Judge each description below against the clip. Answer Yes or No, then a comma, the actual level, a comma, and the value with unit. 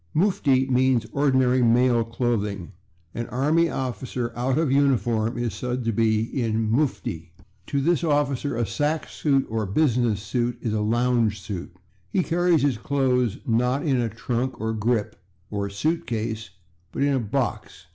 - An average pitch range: Yes, average, 3.4 semitones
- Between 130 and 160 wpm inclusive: Yes, average, 155 wpm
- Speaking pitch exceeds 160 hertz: No, low, 125 Hz